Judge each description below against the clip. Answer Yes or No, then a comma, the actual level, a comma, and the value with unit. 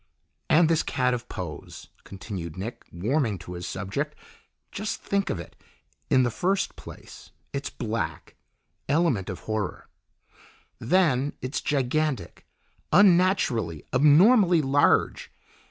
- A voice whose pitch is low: Yes, low, 130 Hz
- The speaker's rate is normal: No, slow, 115 wpm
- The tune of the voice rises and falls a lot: Yes, wide, 7.9 semitones